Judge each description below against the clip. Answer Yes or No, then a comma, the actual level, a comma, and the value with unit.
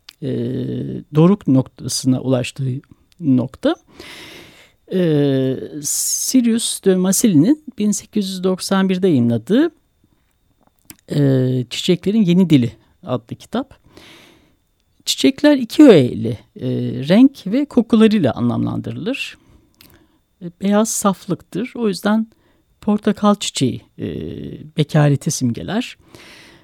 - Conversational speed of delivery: No, slow, 75 wpm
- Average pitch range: No, wide, 8.5 semitones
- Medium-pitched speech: Yes, medium, 175 Hz